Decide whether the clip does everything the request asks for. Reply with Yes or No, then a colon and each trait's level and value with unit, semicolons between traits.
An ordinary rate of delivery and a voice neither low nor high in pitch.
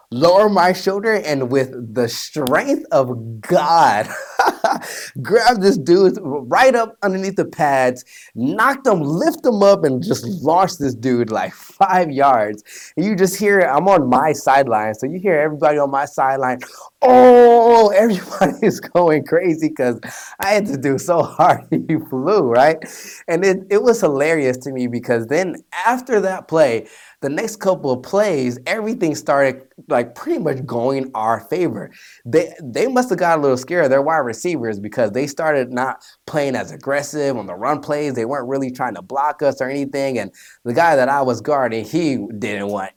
Yes: average, 175 wpm; medium, 150 Hz